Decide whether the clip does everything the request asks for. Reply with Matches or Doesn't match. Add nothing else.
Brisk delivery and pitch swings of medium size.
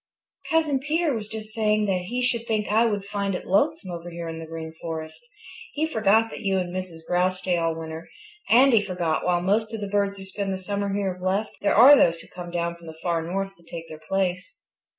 Matches